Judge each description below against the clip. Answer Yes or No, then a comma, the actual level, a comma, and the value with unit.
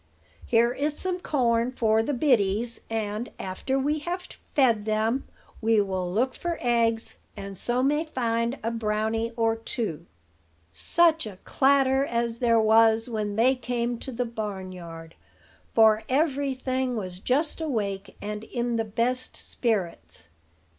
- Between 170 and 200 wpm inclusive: No, average, 140 wpm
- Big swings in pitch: No, average, 3.3 semitones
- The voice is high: Yes, high, 230 Hz